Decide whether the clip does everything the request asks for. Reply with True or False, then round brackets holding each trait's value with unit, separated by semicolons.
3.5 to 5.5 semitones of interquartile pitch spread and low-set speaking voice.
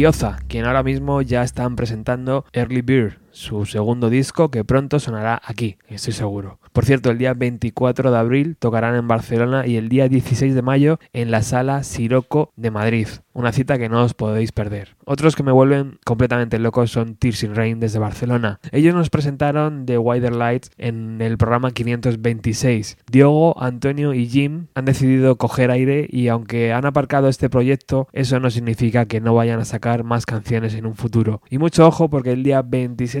False (2.7 semitones; 125 Hz)